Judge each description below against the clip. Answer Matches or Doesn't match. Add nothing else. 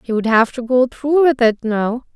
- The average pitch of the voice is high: Matches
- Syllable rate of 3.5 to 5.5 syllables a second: Matches